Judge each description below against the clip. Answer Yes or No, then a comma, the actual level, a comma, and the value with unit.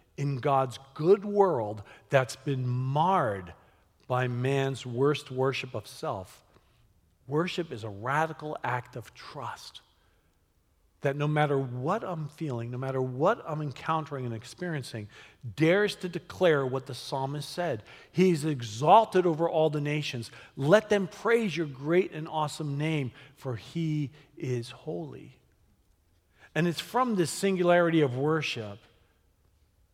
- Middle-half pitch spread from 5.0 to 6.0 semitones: Yes, wide, 5.4 semitones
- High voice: No, low, 135 Hz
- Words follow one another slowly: Yes, slow, 130 wpm